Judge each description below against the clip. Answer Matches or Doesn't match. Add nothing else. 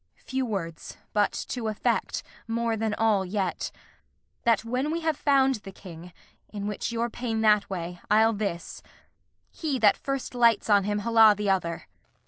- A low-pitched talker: Doesn't match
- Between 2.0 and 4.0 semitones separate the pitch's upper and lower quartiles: Matches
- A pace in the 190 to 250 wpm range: Doesn't match